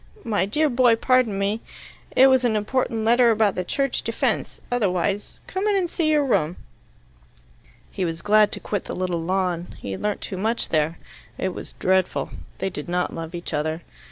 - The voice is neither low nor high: No, high, 205 Hz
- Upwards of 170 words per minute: Yes, average, 185 wpm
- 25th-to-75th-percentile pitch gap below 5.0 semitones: No, average, 5.3 semitones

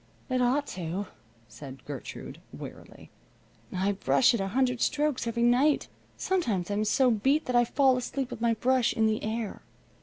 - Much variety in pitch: No, average, 4.1 semitones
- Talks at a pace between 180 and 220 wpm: No, average, 170 wpm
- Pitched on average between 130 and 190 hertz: No, high, 235 Hz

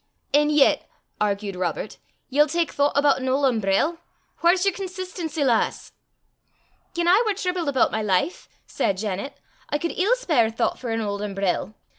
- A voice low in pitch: No, very high, 280 Hz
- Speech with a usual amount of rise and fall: No, wide, 8.4 semitones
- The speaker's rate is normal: Yes, average, 165 wpm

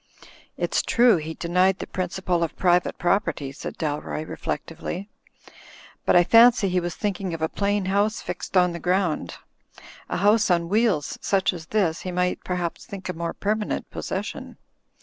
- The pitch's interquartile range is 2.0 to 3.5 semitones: Yes, average, 2.8 semitones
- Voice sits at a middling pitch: Yes, medium, 180 Hz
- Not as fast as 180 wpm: Yes, average, 170 wpm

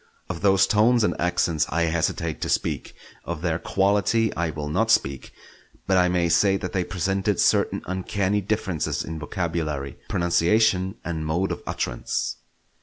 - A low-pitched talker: Yes, very low, 90 Hz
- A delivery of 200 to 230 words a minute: No, average, 155 wpm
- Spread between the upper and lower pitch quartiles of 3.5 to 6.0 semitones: No, average, 3.0 semitones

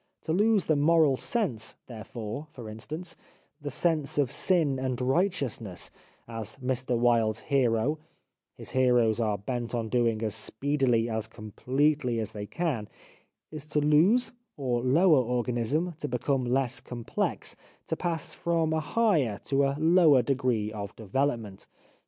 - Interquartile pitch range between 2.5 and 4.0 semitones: No, average, 5.1 semitones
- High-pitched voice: No, low, 130 Hz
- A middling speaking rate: Yes, average, 145 wpm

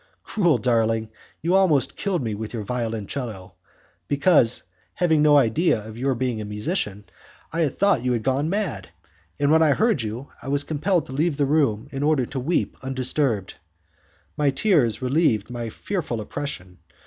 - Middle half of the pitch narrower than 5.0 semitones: No, wide, 5.4 semitones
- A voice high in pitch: No, low, 135 Hz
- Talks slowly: No, average, 165 wpm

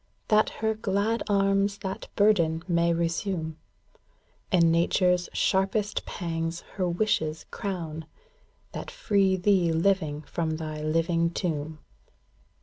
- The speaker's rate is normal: No, slow, 110 wpm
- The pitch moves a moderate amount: Yes, average, 3.4 semitones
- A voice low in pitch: No, medium, 175 Hz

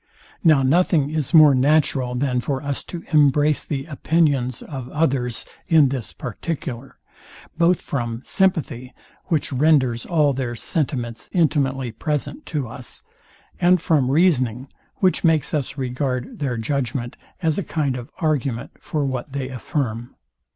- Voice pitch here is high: No, medium, 140 Hz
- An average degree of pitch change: Yes, average, 3.7 semitones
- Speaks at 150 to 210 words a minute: No, slow, 135 wpm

